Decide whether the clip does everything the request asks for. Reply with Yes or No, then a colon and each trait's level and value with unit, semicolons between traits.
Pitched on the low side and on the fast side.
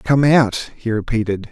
No: low, 120 Hz; slow, 120 wpm